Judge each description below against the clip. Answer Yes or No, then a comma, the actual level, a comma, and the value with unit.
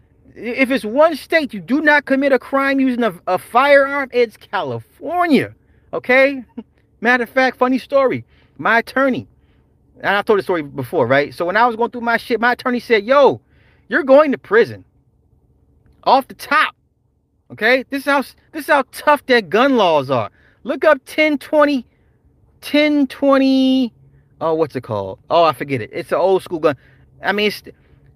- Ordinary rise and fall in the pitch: No, wide, 6.7 semitones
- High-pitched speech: Yes, very high, 250 Hz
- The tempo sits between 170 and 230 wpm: Yes, average, 175 wpm